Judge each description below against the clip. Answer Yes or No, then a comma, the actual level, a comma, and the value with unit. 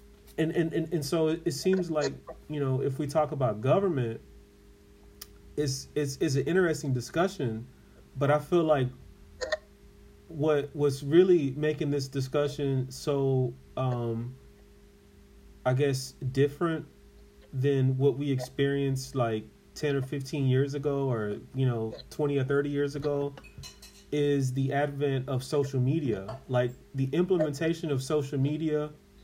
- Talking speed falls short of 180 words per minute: Yes, average, 140 wpm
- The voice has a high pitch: No, medium, 140 Hz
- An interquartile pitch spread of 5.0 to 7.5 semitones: No, average, 2.8 semitones